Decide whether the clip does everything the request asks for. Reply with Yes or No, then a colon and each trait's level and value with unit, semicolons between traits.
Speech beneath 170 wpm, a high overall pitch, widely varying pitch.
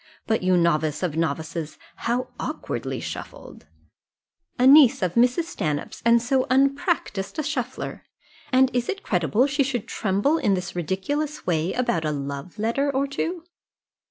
Yes: average, 150 wpm; high, 235 Hz; wide, 8.0 semitones